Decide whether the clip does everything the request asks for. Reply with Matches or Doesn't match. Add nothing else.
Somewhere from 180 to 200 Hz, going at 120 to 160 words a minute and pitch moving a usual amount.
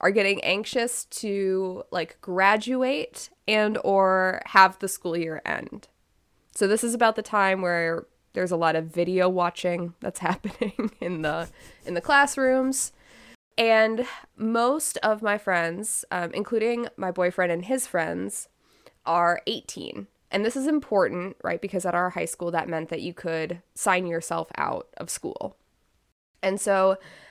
Matches